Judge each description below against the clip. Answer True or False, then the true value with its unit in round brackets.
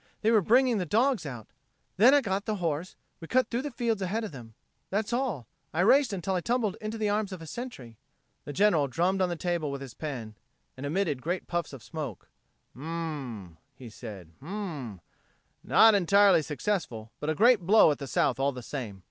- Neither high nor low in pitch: True (175 Hz)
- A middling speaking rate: False (215 wpm)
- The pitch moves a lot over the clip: True (7.5 semitones)